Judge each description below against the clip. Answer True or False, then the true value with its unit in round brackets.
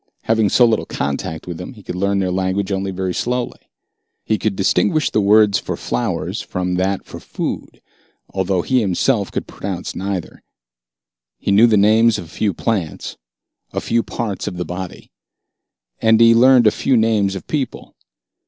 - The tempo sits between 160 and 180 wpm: True (170 wpm)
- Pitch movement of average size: True (3.4 semitones)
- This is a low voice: True (100 Hz)